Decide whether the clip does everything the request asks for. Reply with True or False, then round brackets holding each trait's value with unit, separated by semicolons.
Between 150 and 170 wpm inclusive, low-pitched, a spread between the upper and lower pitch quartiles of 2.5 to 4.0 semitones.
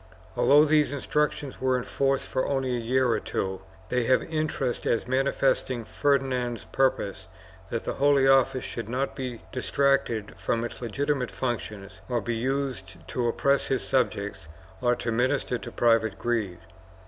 True (160 wpm; 125 Hz; 2.8 semitones)